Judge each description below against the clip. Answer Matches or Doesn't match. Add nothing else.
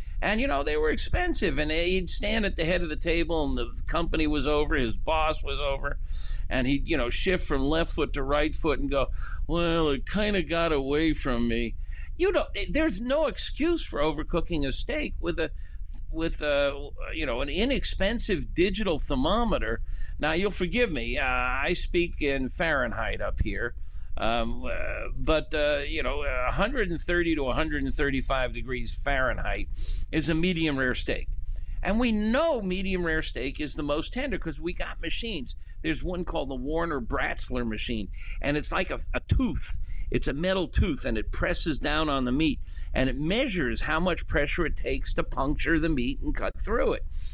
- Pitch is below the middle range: Doesn't match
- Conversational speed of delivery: Matches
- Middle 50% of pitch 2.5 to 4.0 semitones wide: Doesn't match